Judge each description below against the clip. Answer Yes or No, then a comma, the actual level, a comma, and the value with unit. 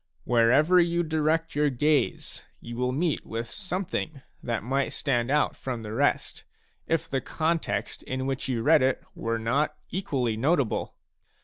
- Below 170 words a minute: Yes, average, 150 wpm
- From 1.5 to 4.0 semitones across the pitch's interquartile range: No, average, 4.8 semitones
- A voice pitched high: No, medium, 140 Hz